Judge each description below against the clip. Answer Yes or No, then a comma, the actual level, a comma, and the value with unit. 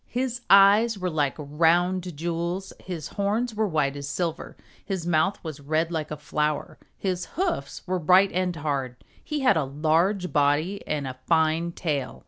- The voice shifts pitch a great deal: No, average, 4.2 semitones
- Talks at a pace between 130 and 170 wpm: Yes, average, 165 wpm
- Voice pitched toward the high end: No, medium, 170 Hz